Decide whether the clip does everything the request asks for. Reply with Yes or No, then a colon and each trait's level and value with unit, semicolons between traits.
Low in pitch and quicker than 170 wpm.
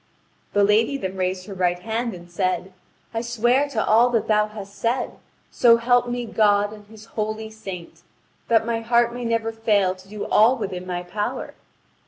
No: high, 215 Hz; average, 185 wpm